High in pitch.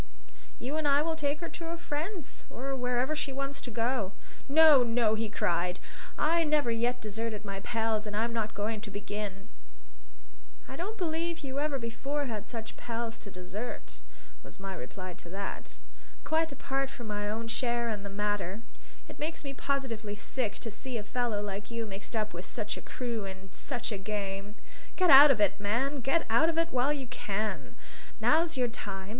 Yes: high, 230 Hz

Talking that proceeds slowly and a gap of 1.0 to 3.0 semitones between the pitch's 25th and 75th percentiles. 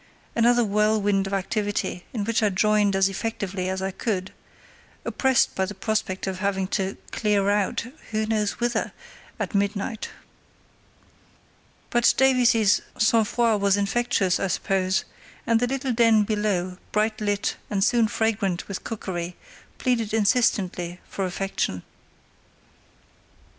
Yes: slow, 125 wpm; average, 2.7 semitones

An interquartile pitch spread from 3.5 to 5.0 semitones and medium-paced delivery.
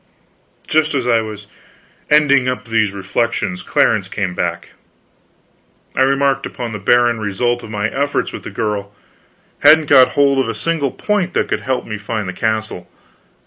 Yes: average, 4.5 semitones; average, 170 wpm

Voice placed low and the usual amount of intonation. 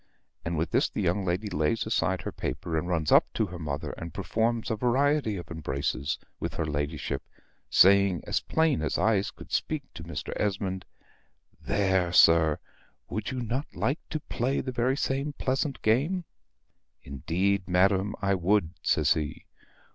No: very low, 95 Hz; wide, 5.8 semitones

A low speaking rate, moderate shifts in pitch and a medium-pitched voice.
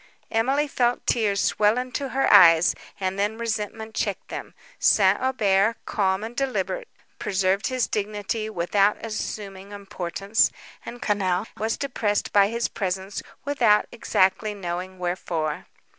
No: slow, 130 wpm; average, 3.1 semitones; high, 205 Hz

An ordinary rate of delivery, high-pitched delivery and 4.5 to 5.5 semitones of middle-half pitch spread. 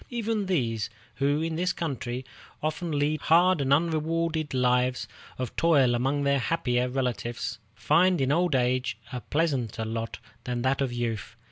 No: average, 150 wpm; medium, 140 Hz; average, 4.8 semitones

